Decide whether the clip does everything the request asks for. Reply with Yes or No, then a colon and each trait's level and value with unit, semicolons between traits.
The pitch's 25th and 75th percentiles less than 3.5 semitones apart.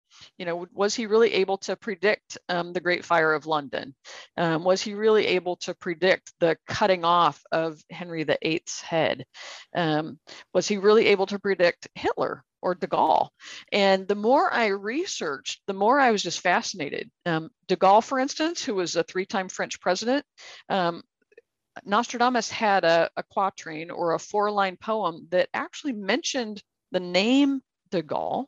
No: average, 3.9 semitones